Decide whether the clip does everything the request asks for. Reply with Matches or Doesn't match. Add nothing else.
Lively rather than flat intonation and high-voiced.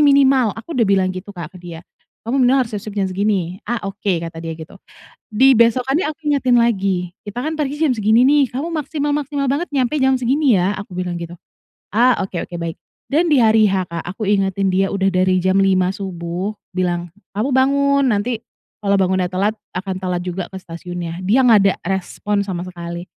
Matches